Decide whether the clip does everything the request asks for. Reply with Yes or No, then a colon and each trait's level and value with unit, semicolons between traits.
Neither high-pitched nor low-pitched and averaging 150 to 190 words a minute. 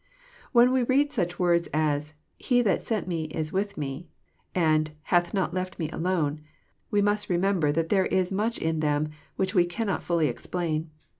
Yes: medium, 175 Hz; average, 180 wpm